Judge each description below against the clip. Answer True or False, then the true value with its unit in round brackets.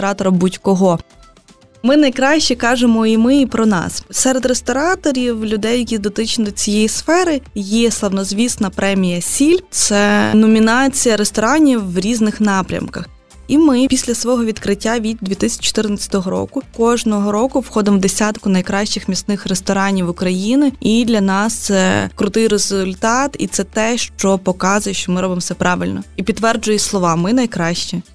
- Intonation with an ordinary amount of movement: True (3.6 semitones)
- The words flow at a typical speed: True (140 wpm)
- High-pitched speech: True (215 Hz)